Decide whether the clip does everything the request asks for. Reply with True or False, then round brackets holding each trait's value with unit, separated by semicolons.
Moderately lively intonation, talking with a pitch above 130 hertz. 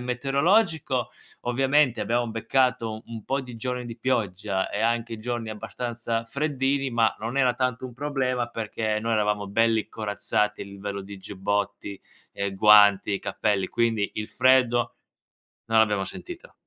False (3.3 semitones; 115 Hz)